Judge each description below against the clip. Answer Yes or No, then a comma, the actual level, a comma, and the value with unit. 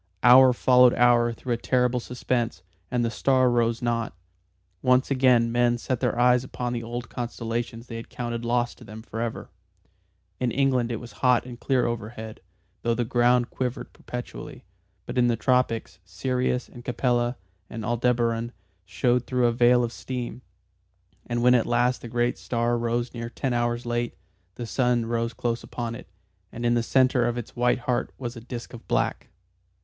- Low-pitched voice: Yes, low, 120 Hz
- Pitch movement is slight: Yes, narrow, 1.0 semitones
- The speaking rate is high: No, average, 175 wpm